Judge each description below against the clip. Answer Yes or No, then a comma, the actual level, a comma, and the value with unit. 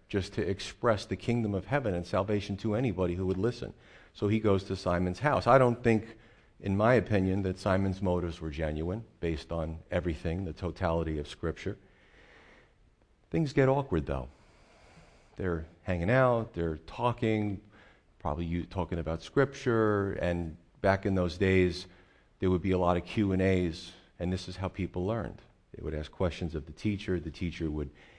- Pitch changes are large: No, average, 3.4 semitones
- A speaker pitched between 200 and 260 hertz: No, very low, 95 Hz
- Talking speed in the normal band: Yes, average, 175 wpm